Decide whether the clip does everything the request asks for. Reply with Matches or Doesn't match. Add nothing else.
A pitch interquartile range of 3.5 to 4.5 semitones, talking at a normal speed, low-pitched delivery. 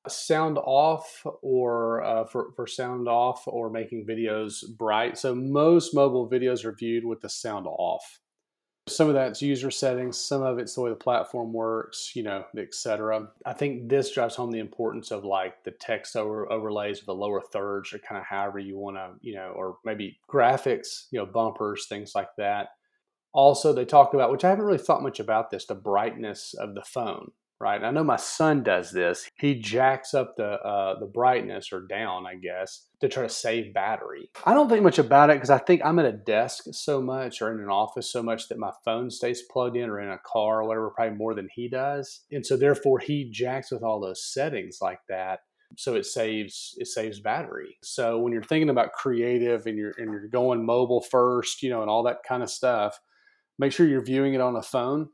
Doesn't match